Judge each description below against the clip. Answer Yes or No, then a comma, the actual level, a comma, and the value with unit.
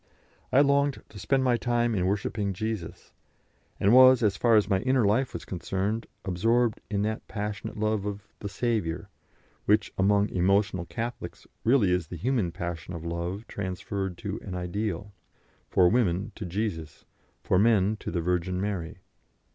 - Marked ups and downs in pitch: No, average, 3.7 semitones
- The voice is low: Yes, low, 100 Hz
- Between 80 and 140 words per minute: No, average, 160 wpm